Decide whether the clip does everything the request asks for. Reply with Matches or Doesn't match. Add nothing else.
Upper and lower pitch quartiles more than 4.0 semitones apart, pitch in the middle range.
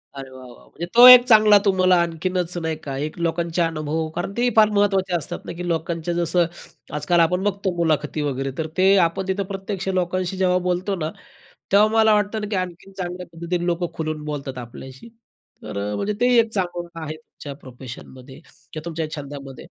Doesn't match